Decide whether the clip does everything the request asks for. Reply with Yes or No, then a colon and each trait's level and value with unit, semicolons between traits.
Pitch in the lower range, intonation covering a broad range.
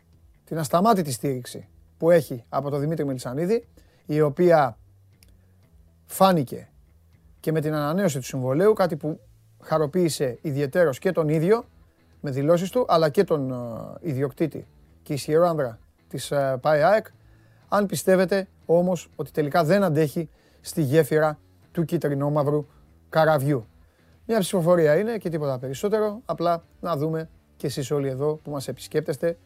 No: medium, 150 Hz; wide, 6.3 semitones